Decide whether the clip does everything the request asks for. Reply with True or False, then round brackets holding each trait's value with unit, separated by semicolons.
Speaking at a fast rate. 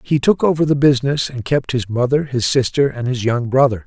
True (235 wpm)